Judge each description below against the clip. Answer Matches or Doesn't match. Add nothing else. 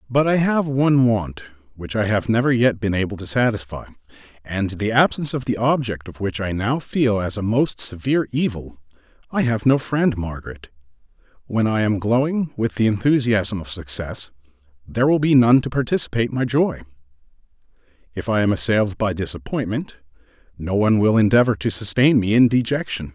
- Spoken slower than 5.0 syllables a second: Doesn't match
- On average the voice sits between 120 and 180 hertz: Doesn't match